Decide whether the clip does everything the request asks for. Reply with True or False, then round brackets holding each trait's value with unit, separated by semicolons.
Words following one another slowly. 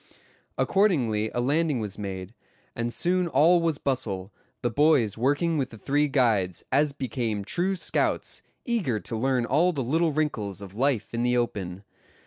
False (160 wpm)